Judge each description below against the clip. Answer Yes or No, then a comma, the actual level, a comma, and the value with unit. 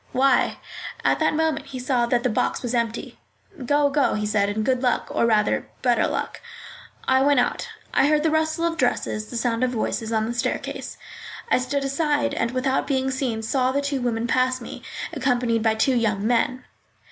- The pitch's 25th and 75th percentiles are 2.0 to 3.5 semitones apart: Yes, average, 3.1 semitones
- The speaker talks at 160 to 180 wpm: No, average, 195 wpm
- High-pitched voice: Yes, very high, 255 Hz